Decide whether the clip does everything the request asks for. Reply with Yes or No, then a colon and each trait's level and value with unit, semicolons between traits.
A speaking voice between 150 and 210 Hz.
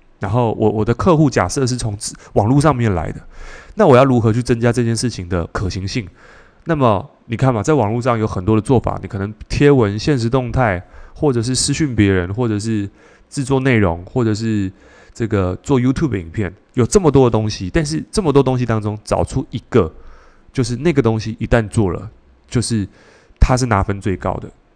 No: low, 115 Hz